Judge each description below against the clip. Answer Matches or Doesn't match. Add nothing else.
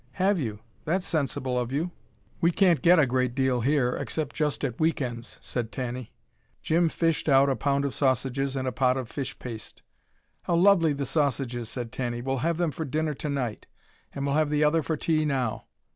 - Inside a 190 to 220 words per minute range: Matches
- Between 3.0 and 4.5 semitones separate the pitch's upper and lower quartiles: Matches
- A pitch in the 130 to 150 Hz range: Matches